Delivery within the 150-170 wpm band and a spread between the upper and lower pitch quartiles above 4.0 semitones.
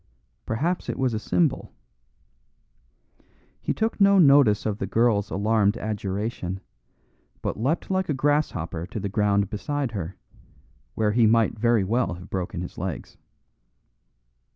No: slow, 135 wpm; average, 5.1 semitones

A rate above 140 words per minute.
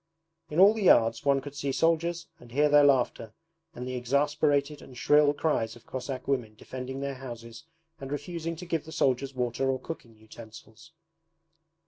Yes: average, 170 wpm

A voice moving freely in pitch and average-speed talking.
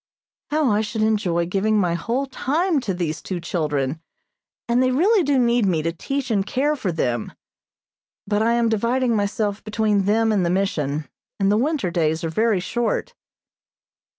Yes: wide, 5.7 semitones; average, 175 wpm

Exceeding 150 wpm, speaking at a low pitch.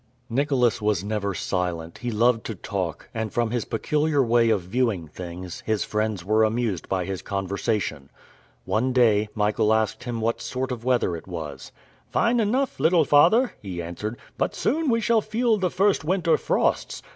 Yes: average, 170 wpm; low, 110 Hz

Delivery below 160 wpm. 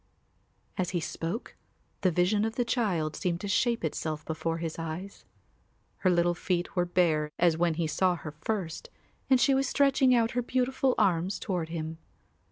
No: average, 175 wpm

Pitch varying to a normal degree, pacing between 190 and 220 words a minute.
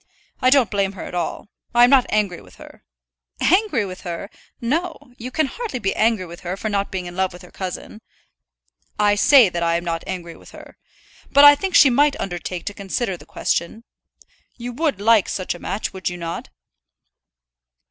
No: wide, 5.9 semitones; average, 200 wpm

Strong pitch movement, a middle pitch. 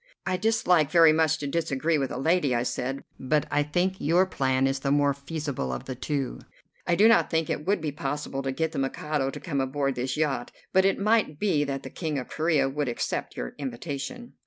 No: average, 3.6 semitones; medium, 145 Hz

